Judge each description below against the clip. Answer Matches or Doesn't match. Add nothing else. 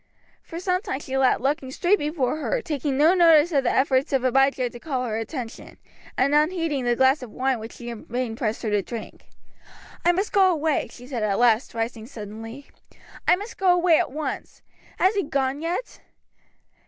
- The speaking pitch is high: Matches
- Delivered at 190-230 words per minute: Matches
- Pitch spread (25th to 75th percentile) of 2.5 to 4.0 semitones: Doesn't match